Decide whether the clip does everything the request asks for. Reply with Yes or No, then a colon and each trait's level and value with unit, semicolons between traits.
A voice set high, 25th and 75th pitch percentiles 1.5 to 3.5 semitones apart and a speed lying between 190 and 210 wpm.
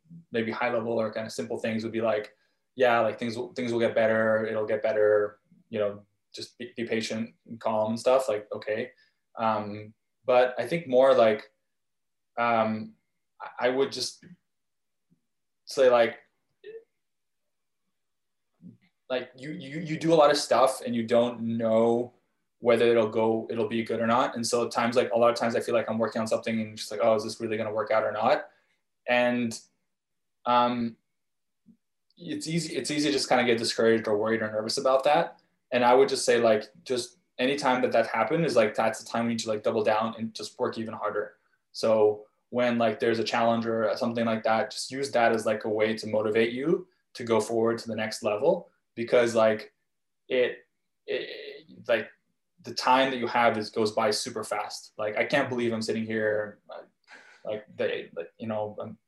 No: low, 115 Hz; narrow, 2.4 semitones; average, 200 wpm